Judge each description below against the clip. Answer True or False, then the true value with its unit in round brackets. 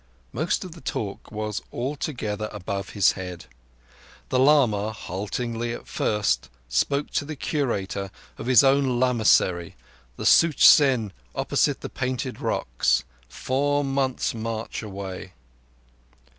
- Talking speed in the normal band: False (120 wpm)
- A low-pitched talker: True (115 Hz)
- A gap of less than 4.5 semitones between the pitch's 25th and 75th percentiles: False (5.2 semitones)